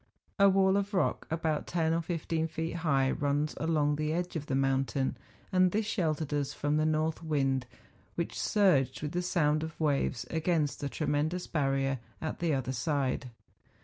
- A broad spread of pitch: No, average, 2.9 semitones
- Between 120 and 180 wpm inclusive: Yes, average, 175 wpm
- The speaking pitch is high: No, medium, 155 Hz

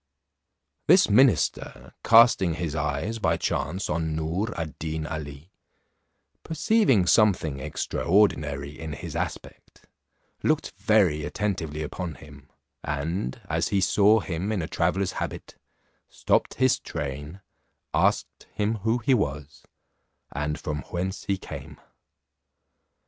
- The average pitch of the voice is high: No, very low, 85 Hz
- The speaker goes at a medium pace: No, slow, 115 wpm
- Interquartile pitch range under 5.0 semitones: No, wide, 5.5 semitones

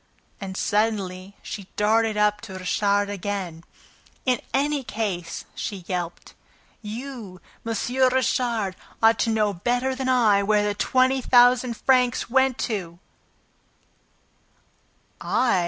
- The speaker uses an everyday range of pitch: Yes, average, 3.7 semitones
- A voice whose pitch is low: No, high, 215 Hz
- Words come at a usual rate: No, slow, 115 wpm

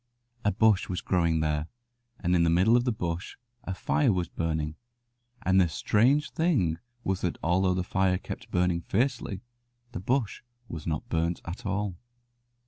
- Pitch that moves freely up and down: No, average, 3.6 semitones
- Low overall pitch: Yes, very low, 90 Hz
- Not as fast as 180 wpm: Yes, average, 170 wpm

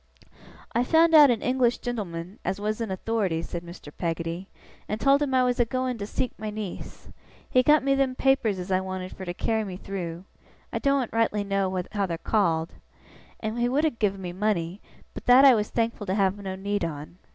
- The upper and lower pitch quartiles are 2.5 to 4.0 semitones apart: No, average, 4.9 semitones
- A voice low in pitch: No, high, 210 Hz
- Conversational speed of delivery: No, fast, 210 wpm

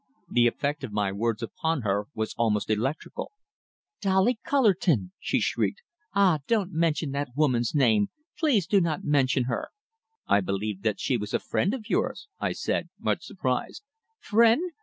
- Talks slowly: No, average, 160 wpm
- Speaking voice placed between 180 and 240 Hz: No, medium, 140 Hz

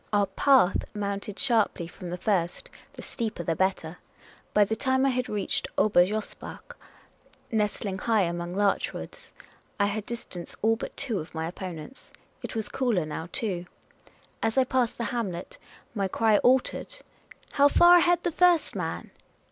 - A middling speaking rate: Yes, average, 170 wpm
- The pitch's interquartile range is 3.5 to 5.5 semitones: Yes, average, 5.1 semitones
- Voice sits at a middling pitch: No, high, 210 Hz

